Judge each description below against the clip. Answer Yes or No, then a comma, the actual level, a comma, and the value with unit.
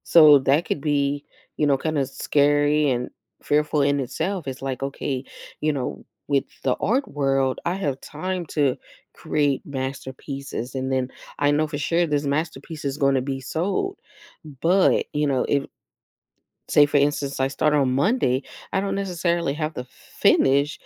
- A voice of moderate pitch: Yes, medium, 145 Hz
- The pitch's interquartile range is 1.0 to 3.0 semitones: Yes, narrow, 2.4 semitones